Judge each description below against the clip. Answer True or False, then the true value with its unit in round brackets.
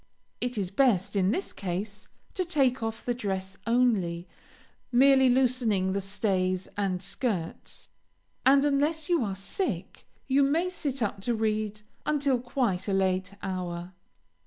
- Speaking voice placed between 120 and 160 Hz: False (215 Hz)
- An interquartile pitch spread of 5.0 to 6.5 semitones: True (5.6 semitones)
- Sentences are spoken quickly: False (140 wpm)